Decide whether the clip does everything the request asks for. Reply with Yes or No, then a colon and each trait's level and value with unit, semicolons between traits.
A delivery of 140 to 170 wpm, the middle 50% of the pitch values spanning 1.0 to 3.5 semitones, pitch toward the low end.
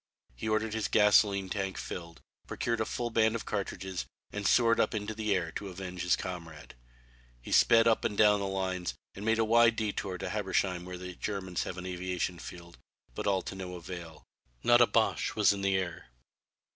No: average, 195 wpm; average, 3.1 semitones; very low, 95 Hz